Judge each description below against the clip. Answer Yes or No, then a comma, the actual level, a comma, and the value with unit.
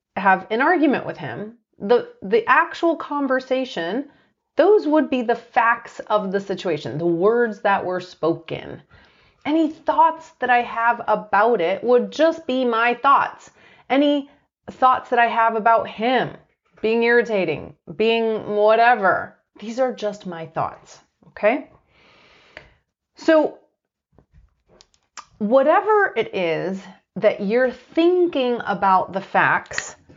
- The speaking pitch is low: No, high, 235 Hz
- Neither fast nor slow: No, slow, 120 wpm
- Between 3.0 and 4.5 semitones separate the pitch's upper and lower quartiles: No, wide, 5.5 semitones